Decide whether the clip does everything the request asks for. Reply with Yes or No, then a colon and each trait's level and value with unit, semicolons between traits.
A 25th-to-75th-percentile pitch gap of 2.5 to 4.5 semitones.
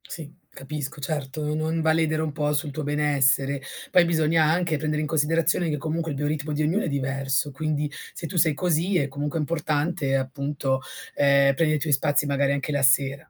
No: narrow, 2.1 semitones